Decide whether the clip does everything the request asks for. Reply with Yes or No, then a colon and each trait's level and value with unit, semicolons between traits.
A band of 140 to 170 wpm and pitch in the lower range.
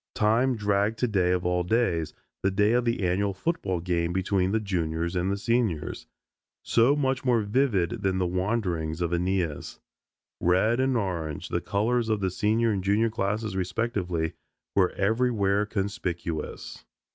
Yes: average, 150 wpm; low, 100 Hz